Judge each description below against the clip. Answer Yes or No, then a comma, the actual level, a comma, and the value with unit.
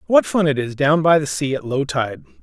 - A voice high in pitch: No, medium, 140 Hz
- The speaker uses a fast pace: Yes, fast, 270 wpm